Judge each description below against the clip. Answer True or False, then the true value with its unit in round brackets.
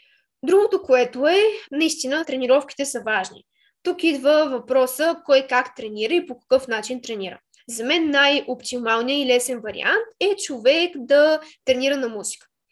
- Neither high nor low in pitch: False (270 Hz)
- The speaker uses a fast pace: False (140 wpm)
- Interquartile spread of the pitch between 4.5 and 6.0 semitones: False (4.0 semitones)